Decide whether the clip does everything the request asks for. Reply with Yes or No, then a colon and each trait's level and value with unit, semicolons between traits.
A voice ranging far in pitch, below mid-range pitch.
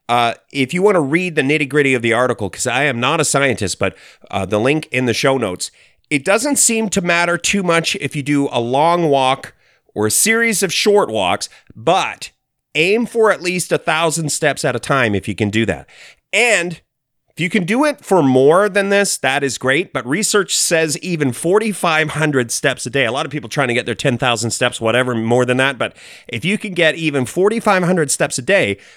No: wide, 6.3 semitones; medium, 150 Hz